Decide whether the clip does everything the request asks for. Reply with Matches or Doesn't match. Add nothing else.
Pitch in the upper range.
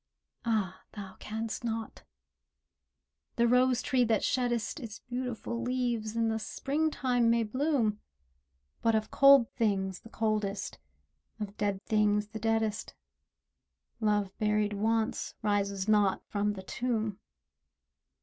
Matches